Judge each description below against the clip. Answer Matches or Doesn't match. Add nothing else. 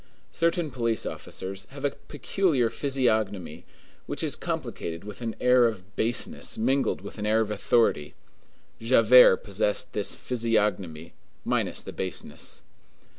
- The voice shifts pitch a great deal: Doesn't match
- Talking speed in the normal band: Doesn't match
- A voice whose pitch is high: Doesn't match